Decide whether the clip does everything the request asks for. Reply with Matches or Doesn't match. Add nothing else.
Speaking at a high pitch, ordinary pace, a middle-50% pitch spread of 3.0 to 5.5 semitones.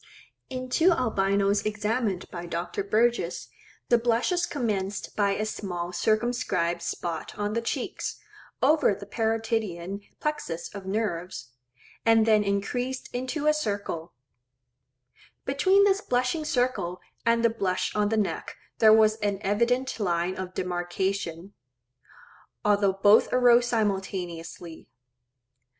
Doesn't match